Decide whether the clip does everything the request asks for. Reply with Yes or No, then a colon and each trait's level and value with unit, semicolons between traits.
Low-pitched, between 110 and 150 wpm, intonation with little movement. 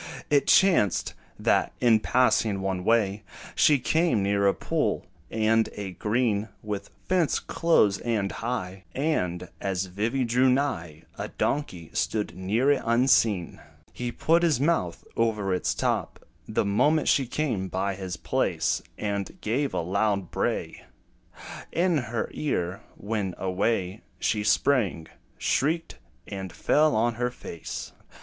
No: low, 110 Hz; slow, 135 wpm; average, 5.0 semitones